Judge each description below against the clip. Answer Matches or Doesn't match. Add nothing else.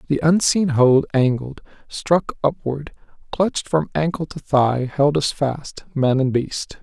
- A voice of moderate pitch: Matches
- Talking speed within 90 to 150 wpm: Matches